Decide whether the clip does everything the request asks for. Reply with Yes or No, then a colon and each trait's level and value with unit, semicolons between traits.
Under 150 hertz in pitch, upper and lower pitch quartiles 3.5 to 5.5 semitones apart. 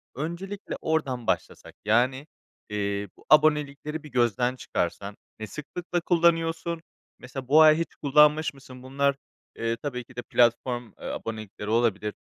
Yes: low, 135 Hz; average, 4.8 semitones